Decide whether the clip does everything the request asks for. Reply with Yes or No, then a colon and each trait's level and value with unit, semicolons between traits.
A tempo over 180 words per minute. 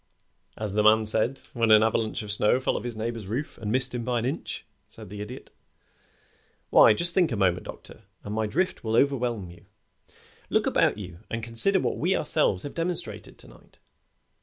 Yes: average, 195 wpm